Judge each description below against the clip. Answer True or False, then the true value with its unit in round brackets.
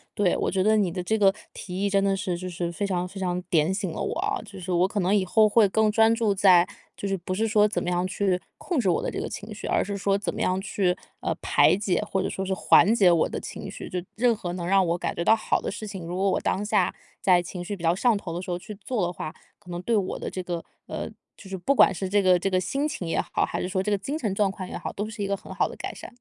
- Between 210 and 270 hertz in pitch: False (195 Hz)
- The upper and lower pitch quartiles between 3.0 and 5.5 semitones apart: False (2.4 semitones)